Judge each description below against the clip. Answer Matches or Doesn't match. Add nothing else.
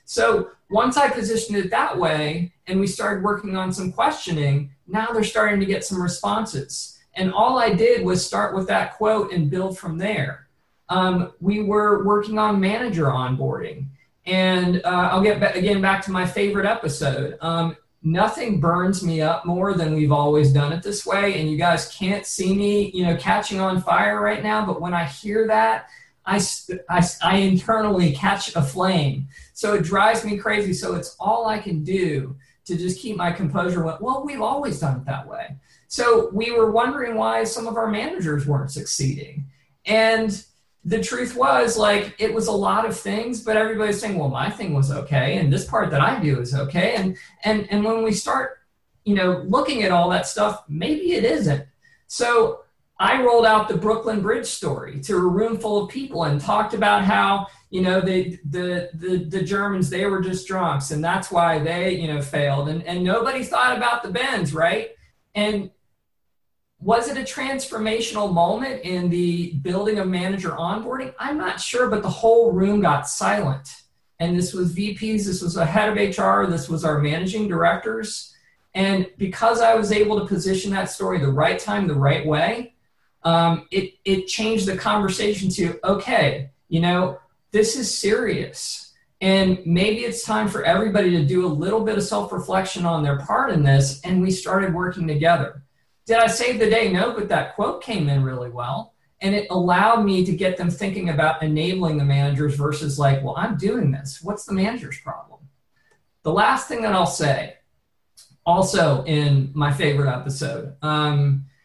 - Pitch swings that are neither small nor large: Matches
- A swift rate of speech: Doesn't match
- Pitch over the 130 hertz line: Matches